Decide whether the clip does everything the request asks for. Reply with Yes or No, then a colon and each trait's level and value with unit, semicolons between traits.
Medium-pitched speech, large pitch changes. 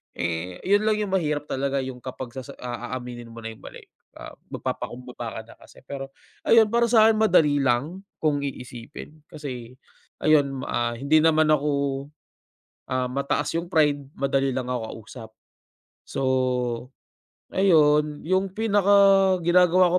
Yes: medium, 145 Hz; wide, 6.4 semitones